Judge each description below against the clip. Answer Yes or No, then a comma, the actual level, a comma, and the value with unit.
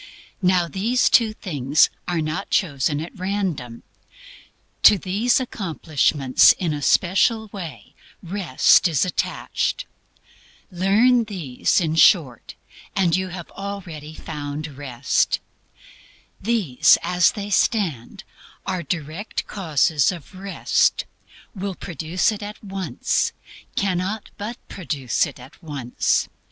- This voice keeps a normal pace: No, slow, 110 wpm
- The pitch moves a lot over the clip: No, average, 4.9 semitones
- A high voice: No, medium, 180 Hz